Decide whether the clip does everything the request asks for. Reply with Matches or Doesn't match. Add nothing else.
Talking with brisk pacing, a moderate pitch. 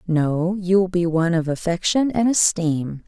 Doesn't match